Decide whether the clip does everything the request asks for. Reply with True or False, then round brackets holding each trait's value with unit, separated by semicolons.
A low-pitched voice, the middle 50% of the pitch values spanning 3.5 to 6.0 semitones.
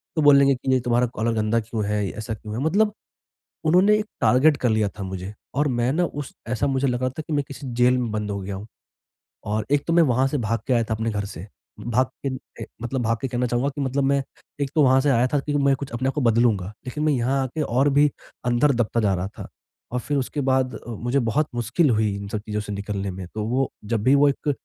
True (125 Hz; 4.2 semitones)